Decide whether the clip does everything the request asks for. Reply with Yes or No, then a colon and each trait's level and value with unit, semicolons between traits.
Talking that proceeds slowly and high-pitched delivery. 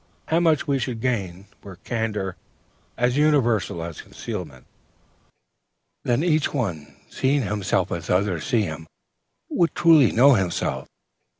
No: slow, 125 wpm; low, 115 Hz